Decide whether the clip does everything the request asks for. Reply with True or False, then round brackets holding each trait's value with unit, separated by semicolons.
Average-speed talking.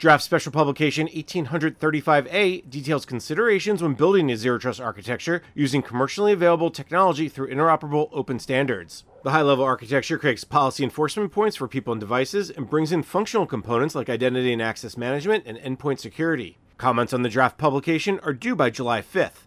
True (170 wpm)